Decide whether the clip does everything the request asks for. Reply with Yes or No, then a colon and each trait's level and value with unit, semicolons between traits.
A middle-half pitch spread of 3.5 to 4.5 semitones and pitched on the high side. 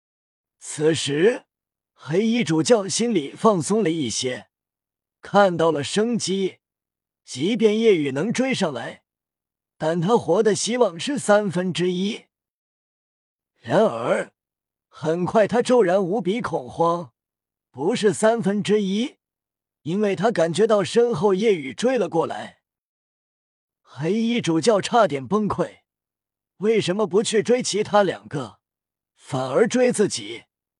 No: wide, 5.5 semitones; high, 195 Hz